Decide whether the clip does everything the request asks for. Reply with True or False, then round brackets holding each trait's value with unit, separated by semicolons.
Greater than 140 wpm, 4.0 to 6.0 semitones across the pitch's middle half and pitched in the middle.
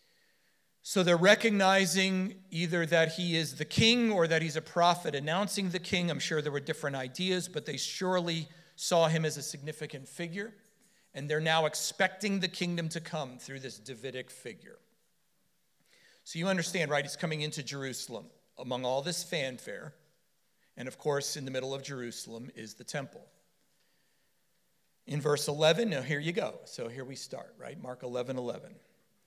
True (170 wpm; 4.7 semitones; 160 Hz)